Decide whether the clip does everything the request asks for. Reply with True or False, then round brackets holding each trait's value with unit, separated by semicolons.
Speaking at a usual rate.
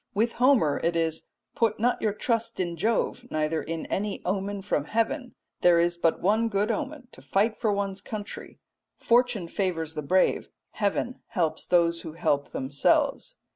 True (165 wpm)